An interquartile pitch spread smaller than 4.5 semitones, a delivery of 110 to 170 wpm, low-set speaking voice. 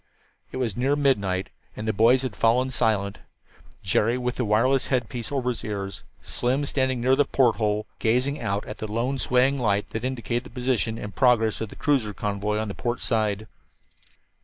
No: average, 3.4 semitones; average, 185 wpm; low, 115 Hz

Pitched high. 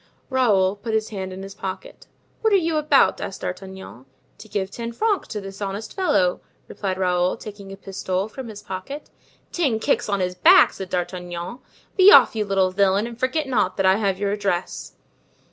Yes: high, 200 Hz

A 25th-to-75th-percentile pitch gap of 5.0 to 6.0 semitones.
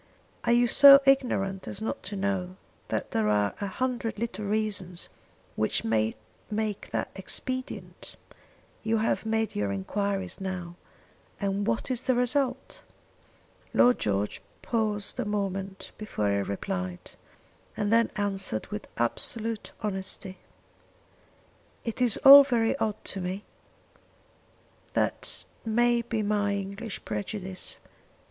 No: average, 3.5 semitones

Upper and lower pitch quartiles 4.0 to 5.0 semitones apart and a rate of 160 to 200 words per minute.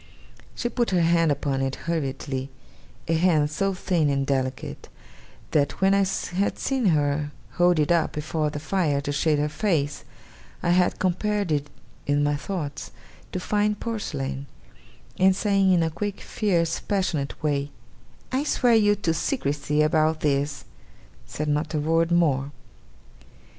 No: average, 4.5 semitones; average, 150 wpm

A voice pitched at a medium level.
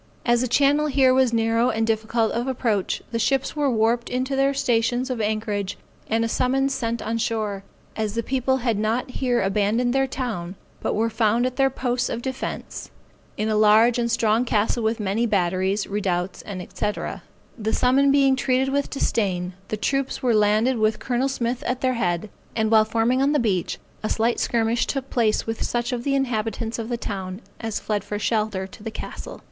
No: high, 230 Hz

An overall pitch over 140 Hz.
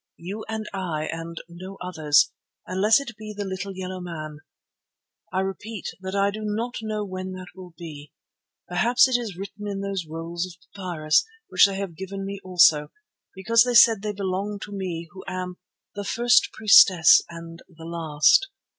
Yes: high, 190 Hz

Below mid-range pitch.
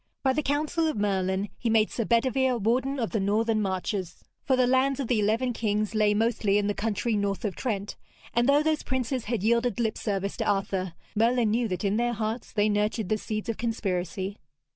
No: high, 220 Hz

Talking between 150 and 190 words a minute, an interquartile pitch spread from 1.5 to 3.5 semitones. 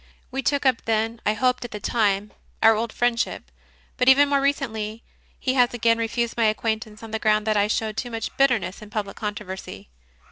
No: fast, 205 wpm; narrow, 2.4 semitones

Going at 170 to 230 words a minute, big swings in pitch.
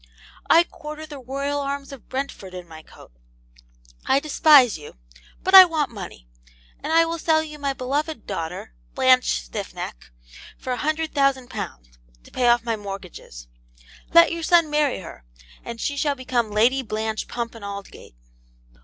No: average, 160 wpm; wide, 6.4 semitones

